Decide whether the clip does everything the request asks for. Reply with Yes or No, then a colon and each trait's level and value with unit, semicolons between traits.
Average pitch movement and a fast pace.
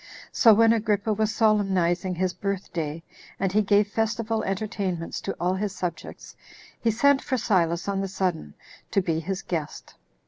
No: average, 3.2 semitones; average, 165 wpm